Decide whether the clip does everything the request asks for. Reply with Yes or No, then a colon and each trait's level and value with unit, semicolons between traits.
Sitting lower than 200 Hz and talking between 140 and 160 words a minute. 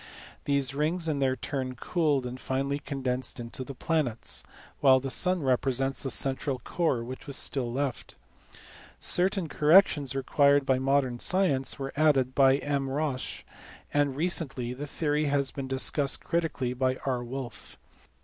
Yes: low, 135 Hz; average, 150 wpm